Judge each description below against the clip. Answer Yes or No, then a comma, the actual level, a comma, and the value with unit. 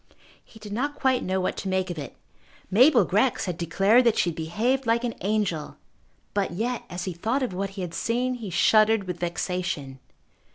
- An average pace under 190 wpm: No, average, 200 wpm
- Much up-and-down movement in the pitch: No, average, 4.7 semitones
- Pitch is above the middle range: Yes, high, 200 Hz